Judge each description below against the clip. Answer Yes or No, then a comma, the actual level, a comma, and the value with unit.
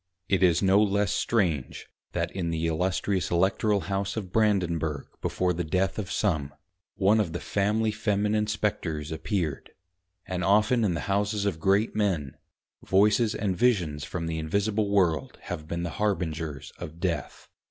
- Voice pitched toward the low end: Yes, very low, 95 Hz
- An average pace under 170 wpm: Yes, average, 155 wpm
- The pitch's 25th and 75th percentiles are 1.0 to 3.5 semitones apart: No, average, 4.0 semitones